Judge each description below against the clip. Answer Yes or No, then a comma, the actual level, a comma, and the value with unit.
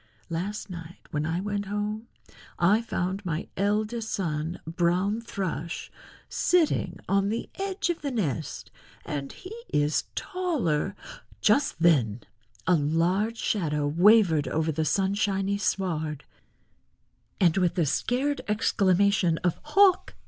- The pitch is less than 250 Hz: Yes, high, 190 Hz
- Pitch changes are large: No, average, 4.6 semitones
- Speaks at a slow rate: Yes, slow, 120 wpm